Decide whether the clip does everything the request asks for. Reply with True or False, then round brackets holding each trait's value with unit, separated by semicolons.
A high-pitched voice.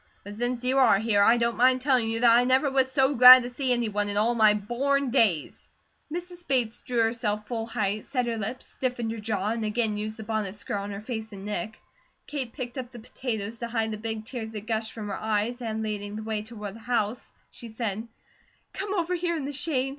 True (230 Hz)